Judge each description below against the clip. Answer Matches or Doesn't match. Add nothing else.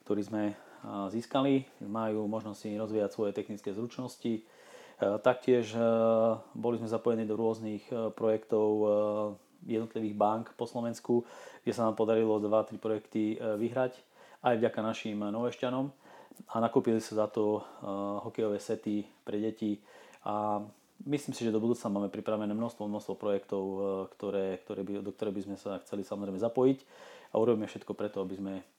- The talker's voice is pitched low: Matches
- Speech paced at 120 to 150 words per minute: Matches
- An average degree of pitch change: Doesn't match